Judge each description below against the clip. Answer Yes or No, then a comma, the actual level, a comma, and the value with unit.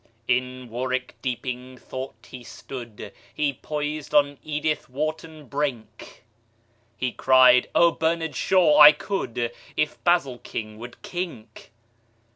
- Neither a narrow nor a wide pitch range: Yes, average, 3.5 semitones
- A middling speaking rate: No, slow, 95 wpm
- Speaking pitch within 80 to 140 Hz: Yes, low, 135 Hz